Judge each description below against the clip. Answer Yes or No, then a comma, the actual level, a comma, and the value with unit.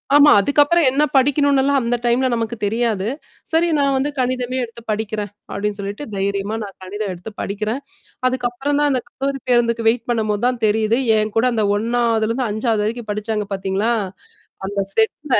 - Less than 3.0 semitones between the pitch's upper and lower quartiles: No, average, 3.6 semitones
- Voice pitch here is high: Yes, high, 230 Hz